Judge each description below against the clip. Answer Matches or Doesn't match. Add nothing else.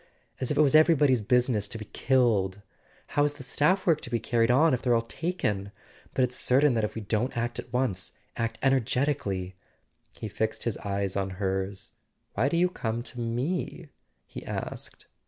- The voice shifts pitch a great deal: Doesn't match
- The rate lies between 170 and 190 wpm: Matches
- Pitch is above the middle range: Doesn't match